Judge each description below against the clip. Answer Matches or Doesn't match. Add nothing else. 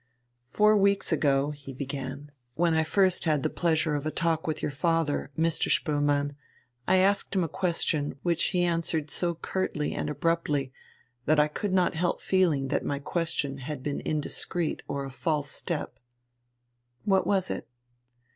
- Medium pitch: Matches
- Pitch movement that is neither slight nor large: Matches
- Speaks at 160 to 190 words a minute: Matches